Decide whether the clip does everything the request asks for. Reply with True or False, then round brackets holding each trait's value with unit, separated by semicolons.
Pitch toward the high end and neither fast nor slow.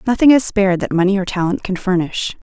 False (195 Hz; 215 wpm)